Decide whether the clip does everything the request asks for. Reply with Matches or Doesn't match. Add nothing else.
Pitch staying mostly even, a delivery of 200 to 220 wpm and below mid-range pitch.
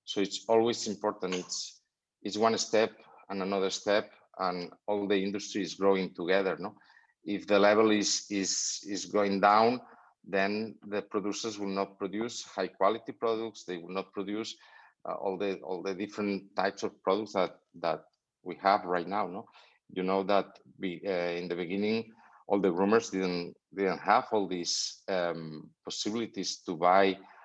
Doesn't match